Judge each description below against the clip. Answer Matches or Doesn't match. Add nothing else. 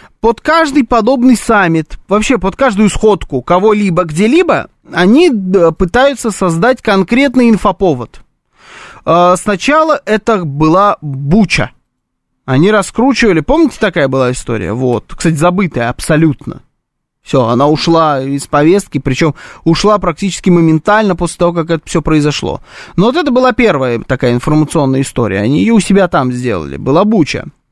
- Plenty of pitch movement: Matches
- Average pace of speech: Matches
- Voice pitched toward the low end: Doesn't match